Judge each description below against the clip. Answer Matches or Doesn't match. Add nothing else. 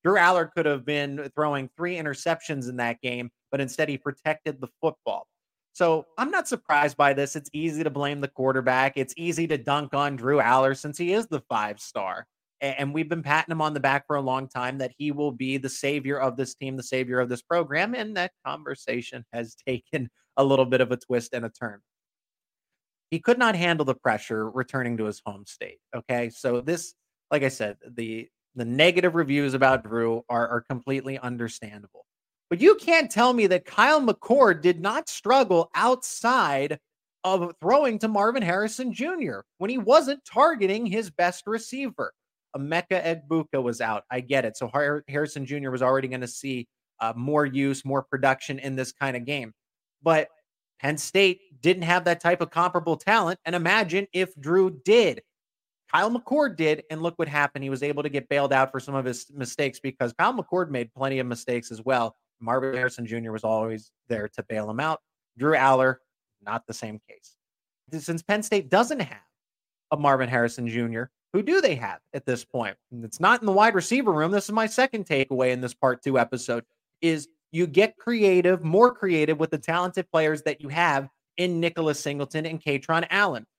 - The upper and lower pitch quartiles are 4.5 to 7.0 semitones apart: Matches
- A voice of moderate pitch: Matches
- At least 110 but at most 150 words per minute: Doesn't match